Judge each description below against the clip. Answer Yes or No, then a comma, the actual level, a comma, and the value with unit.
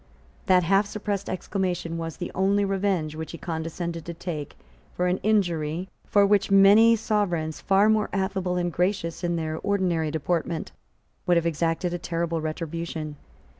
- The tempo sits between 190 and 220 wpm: No, average, 155 wpm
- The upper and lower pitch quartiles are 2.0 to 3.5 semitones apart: Yes, average, 3.0 semitones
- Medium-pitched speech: Yes, medium, 175 Hz